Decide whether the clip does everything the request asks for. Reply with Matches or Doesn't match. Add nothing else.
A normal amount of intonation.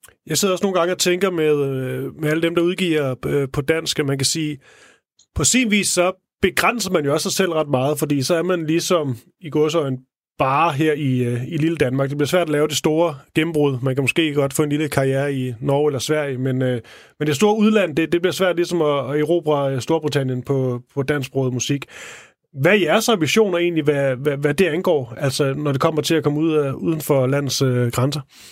Matches